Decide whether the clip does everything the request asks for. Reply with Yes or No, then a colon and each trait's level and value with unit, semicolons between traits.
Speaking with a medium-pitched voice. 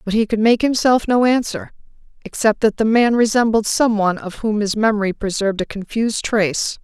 No: high, 215 Hz